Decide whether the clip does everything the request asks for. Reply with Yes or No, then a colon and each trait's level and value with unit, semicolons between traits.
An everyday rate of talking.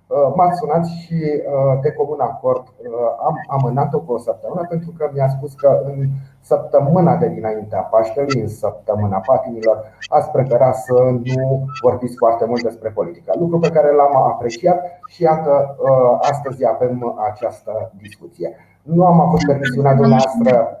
Yes: average, 140 wpm